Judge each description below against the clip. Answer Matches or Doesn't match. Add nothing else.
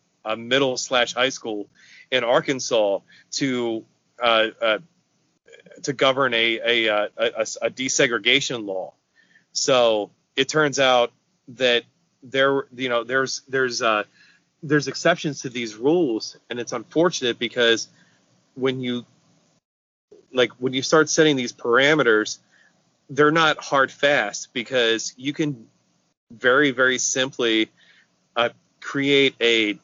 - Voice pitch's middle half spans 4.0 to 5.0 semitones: Doesn't match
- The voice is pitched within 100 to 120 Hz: Doesn't match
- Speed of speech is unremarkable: Doesn't match